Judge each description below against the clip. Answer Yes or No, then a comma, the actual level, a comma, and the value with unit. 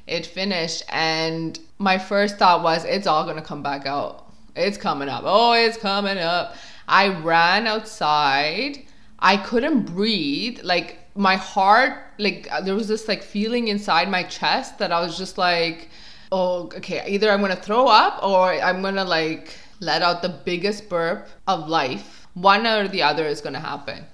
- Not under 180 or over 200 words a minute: No, average, 170 wpm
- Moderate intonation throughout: Yes, average, 3.5 semitones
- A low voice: No, medium, 185 Hz